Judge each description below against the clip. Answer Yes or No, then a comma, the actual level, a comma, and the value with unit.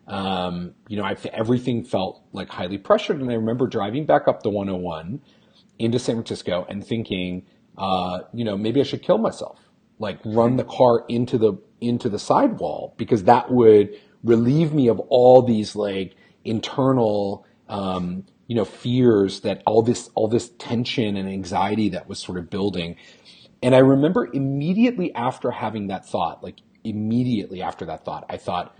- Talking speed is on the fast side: No, average, 170 wpm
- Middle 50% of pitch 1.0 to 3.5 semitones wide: No, average, 4.1 semitones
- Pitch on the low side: Yes, low, 110 Hz